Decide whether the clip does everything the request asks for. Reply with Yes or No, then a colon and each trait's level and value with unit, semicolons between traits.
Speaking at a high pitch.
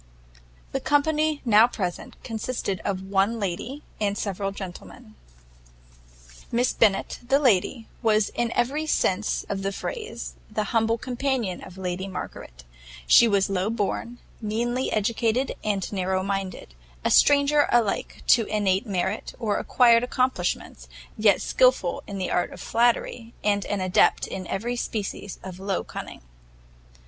Yes: high, 215 Hz